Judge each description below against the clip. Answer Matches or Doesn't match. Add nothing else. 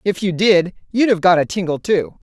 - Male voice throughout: Doesn't match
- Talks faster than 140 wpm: Matches